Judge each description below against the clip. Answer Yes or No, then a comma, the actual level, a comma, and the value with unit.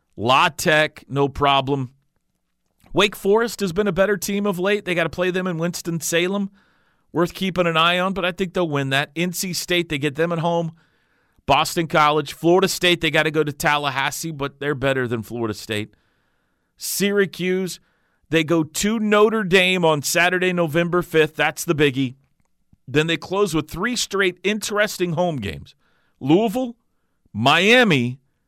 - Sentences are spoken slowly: No, average, 165 wpm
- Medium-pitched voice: Yes, medium, 170 Hz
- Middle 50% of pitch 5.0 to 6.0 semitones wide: No, average, 4.2 semitones